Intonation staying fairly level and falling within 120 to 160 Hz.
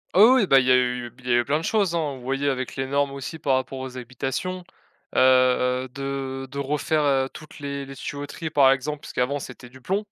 Yes: narrow, 2.1 semitones; low, 135 Hz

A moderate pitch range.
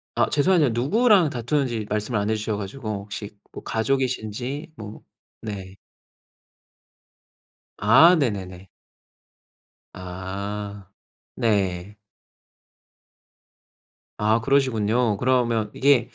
Yes: average, 4.1 semitones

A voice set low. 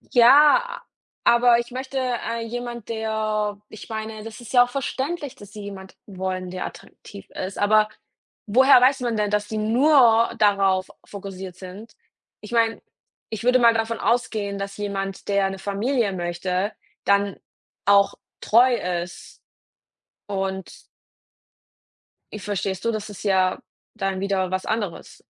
No: high, 210 Hz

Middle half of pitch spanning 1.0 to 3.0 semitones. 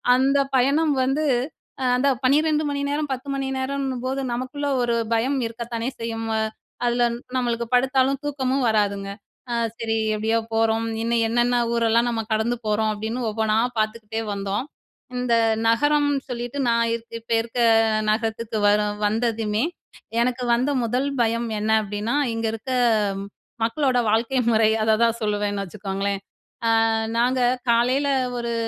Yes: average, 2.7 semitones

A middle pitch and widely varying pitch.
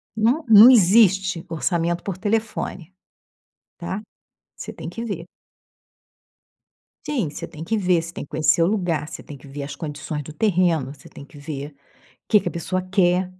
No: medium, 175 Hz; average, 4.8 semitones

